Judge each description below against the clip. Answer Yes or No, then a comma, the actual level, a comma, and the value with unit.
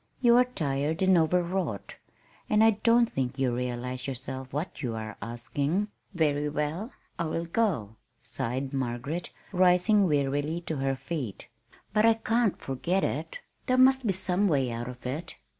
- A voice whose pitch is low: No, medium, 155 Hz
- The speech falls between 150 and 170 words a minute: Yes, average, 160 wpm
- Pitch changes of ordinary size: No, wide, 6.7 semitones